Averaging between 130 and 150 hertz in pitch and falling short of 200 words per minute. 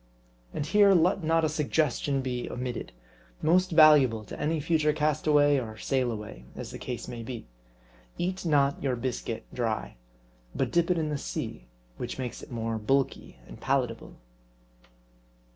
Yes: medium, 140 Hz; average, 150 wpm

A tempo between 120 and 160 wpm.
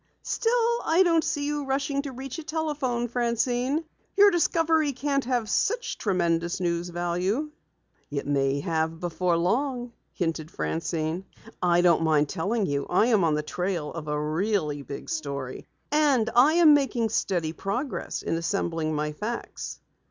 Yes: average, 150 wpm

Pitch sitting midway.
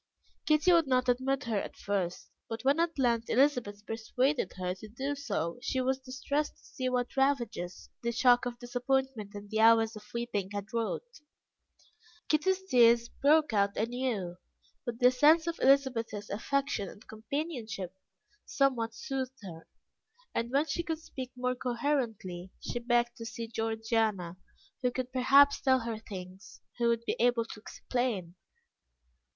No: high, 240 Hz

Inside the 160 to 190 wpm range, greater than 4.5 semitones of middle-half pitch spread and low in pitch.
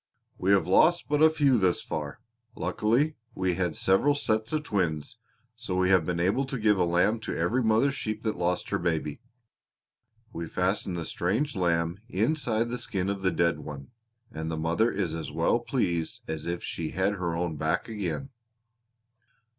Yes: average, 180 wpm; average, 5.1 semitones; very low, 95 Hz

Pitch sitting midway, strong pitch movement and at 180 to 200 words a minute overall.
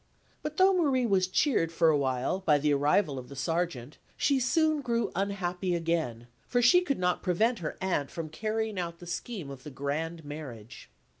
Yes: medium, 175 Hz; wide, 7.2 semitones; average, 190 wpm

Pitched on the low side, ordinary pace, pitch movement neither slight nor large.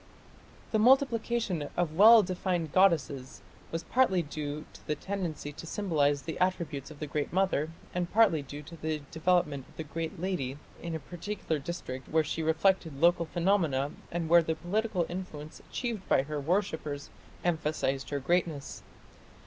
No: medium, 165 Hz; average, 155 wpm; average, 3.8 semitones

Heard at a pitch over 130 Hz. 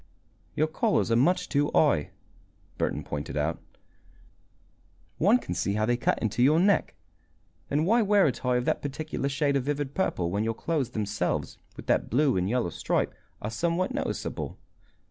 Yes: medium, 140 Hz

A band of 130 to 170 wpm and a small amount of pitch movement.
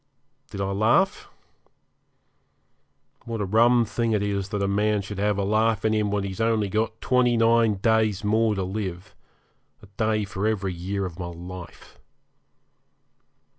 Yes: average, 160 wpm; narrow, 2.2 semitones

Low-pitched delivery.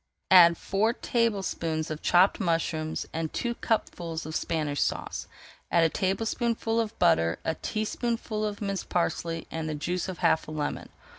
No: medium, 175 Hz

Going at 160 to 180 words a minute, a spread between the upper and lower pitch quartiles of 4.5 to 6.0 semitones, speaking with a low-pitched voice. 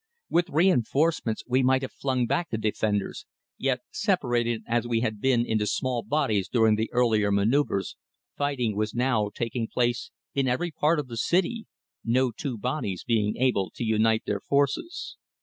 No: average, 165 wpm; average, 3.9 semitones; low, 120 Hz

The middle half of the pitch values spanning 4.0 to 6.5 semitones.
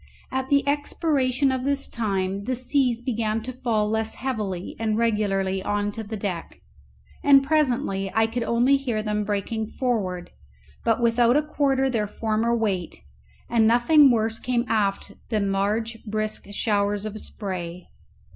No: average, 3.5 semitones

